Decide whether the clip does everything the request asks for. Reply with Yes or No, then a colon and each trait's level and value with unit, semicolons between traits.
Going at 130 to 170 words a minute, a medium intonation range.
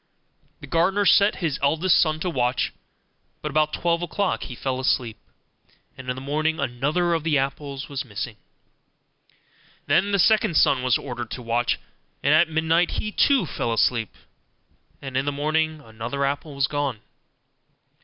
Yes: average, 160 wpm; average, 4.0 semitones